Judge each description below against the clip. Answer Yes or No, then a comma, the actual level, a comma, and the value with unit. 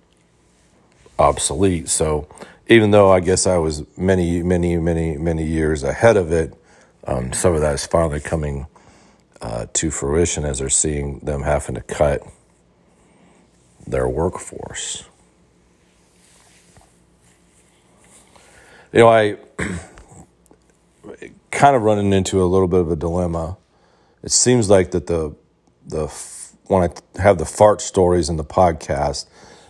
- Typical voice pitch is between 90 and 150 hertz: No, very low, 80 Hz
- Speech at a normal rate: No, slow, 125 wpm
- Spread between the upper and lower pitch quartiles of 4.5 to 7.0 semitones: Yes, wide, 5.4 semitones